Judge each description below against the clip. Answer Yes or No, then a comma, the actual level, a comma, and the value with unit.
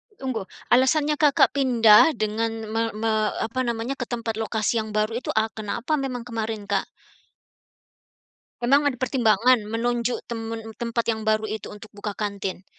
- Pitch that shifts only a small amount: Yes, narrow, 2.3 semitones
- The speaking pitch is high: Yes, high, 225 Hz